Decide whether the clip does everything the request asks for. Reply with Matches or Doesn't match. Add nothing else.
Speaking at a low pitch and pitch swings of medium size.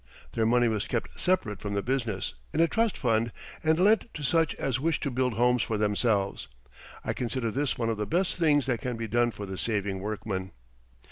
Matches